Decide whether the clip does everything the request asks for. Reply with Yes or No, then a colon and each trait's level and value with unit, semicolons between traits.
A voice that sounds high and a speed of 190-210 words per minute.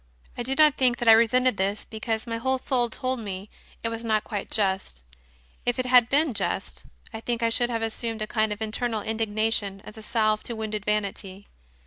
Yes: high, 225 Hz; fast, 205 wpm